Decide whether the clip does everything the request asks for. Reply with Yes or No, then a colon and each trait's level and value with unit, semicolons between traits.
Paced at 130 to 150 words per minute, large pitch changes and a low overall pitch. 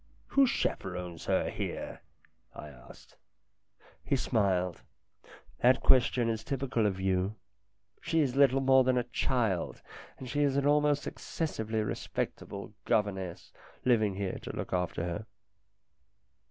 Yes: slow, 135 wpm; wide, 5.8 semitones; low, 110 Hz